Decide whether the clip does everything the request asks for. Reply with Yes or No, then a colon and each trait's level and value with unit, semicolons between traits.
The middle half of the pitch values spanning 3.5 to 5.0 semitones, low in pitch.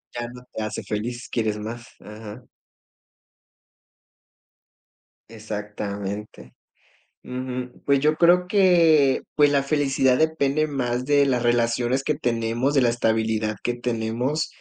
Yes: average, 4.1 semitones; low, 125 Hz